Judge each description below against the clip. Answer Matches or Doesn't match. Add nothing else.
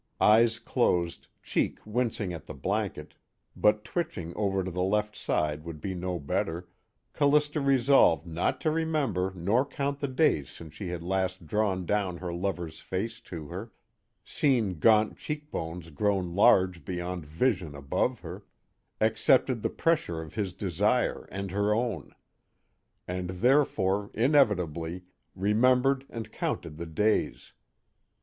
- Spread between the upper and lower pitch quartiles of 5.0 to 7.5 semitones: Matches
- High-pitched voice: Doesn't match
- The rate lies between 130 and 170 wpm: Matches